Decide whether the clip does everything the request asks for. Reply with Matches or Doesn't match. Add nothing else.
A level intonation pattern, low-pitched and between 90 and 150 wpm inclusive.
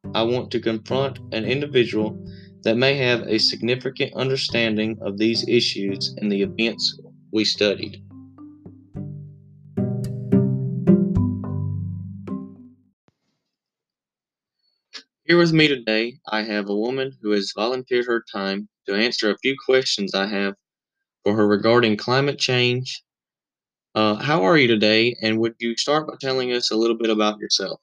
Doesn't match